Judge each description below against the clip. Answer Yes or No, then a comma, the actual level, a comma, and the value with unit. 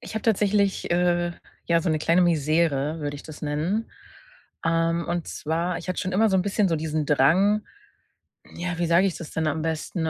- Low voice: No, medium, 170 Hz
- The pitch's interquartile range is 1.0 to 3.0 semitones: Yes, narrow, 2.6 semitones